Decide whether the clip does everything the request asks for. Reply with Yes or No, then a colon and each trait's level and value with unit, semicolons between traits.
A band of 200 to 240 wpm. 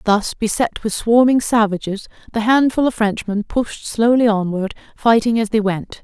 No: average, 160 wpm